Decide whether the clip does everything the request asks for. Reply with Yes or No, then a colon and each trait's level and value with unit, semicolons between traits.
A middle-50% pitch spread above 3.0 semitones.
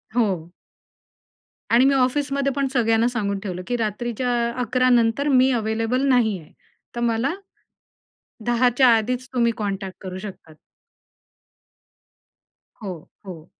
Yes: average, 3.6 semitones